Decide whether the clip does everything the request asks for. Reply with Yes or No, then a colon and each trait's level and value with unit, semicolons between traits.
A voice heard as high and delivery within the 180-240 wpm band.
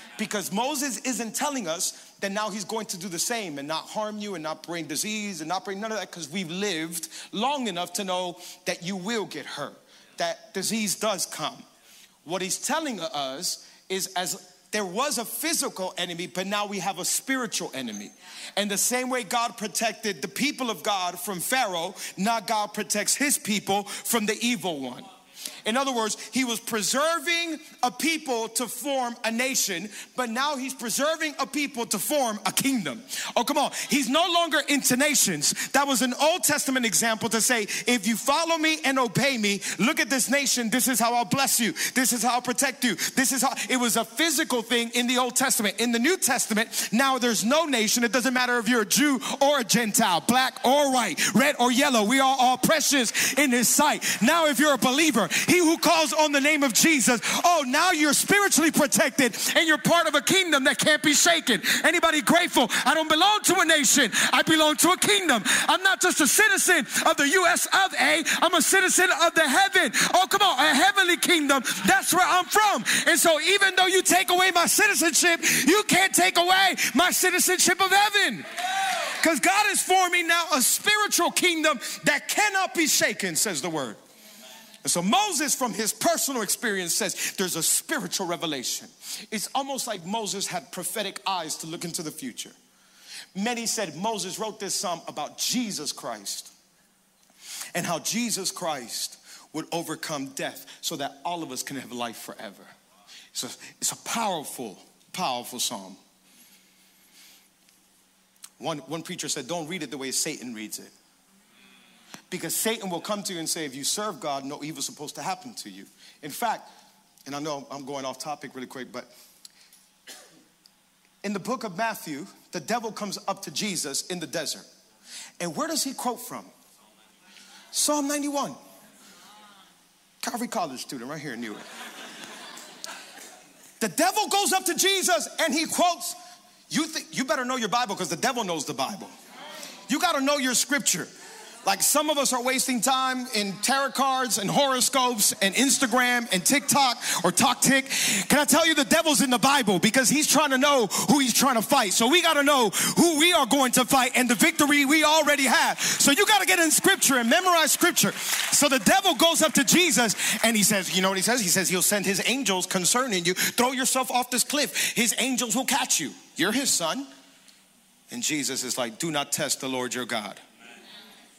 Yes: very high, 250 Hz; average, 195 wpm